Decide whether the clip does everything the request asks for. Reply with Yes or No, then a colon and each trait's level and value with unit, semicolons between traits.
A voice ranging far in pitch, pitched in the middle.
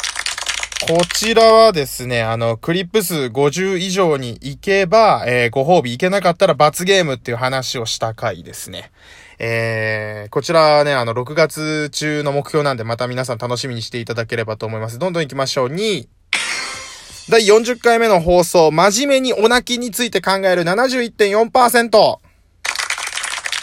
Yes: wide, 8.3 semitones; medium, 155 Hz